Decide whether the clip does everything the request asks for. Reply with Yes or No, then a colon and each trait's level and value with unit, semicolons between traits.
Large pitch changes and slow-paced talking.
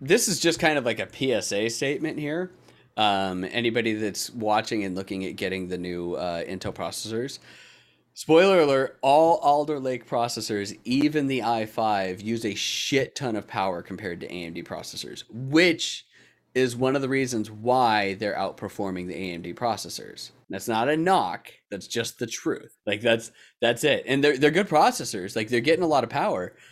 No: wide, 5.9 semitones; average, 175 wpm